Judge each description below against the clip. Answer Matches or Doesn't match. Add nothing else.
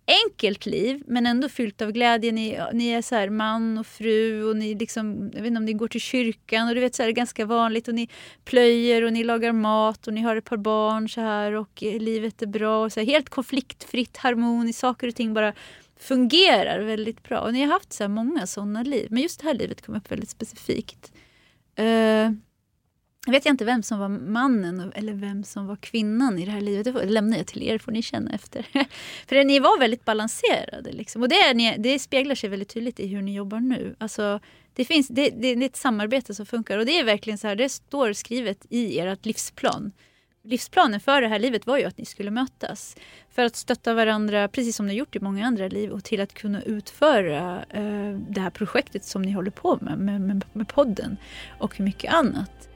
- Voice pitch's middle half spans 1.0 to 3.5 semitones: Matches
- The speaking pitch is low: Doesn't match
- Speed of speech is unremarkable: Doesn't match